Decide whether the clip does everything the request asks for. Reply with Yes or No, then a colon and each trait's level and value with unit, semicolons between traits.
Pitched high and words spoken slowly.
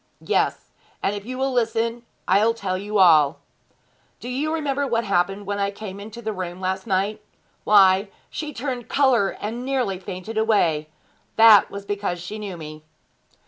No: high, 205 Hz; average, 165 wpm